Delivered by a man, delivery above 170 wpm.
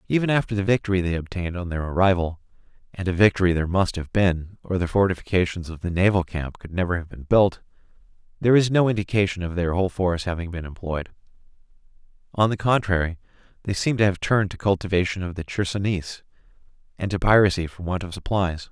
Yes: male; average, 185 wpm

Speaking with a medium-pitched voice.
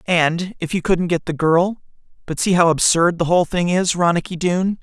Yes: medium, 175 Hz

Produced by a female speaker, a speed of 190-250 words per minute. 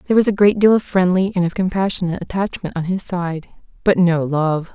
Yes: female; average, 200 wpm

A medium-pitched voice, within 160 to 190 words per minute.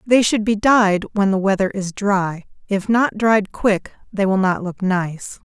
No: high, 200 Hz; average, 185 wpm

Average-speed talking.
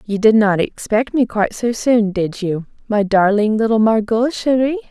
Yes: average, 185 wpm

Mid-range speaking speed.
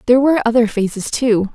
Yes: average, 195 wpm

